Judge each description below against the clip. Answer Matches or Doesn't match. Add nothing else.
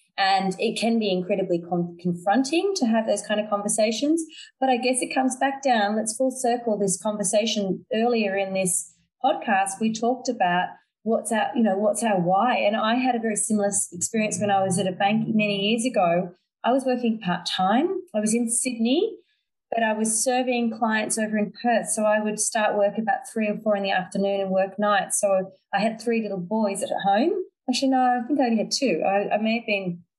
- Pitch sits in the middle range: Doesn't match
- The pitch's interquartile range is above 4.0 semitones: Doesn't match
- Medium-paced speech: Doesn't match